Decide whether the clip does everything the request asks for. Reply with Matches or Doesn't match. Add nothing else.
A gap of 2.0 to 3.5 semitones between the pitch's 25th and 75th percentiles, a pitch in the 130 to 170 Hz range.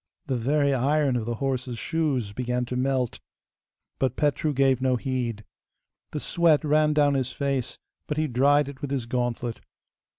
Matches